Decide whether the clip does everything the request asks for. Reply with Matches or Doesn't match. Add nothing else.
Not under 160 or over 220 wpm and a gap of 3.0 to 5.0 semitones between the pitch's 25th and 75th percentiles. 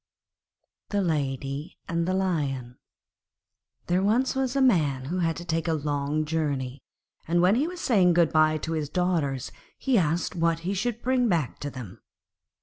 Matches